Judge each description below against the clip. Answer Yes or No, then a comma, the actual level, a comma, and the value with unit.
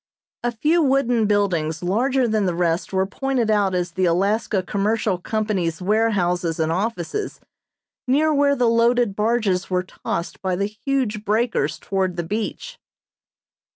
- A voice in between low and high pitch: No, high, 210 Hz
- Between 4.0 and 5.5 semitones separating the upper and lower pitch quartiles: Yes, average, 4.5 semitones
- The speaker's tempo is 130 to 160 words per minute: Yes, average, 145 wpm